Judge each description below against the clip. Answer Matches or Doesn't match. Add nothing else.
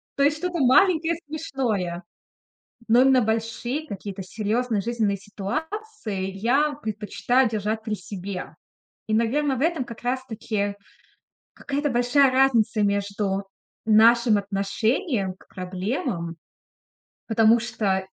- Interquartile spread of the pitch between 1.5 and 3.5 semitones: Doesn't match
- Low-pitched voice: Doesn't match